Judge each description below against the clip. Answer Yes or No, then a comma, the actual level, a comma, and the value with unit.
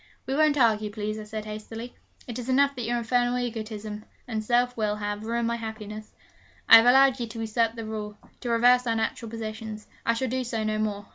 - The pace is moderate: No, fast, 215 wpm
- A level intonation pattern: Yes, narrow, 2.1 semitones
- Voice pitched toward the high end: Yes, high, 225 Hz